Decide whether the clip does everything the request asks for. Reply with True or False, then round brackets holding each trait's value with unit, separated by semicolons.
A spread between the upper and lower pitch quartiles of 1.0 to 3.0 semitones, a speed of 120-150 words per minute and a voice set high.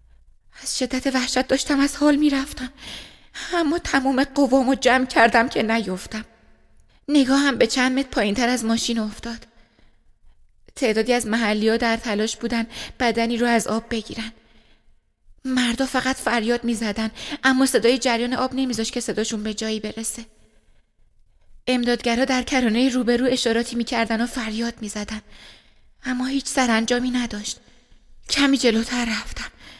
True (2.5 semitones; 140 wpm; 240 Hz)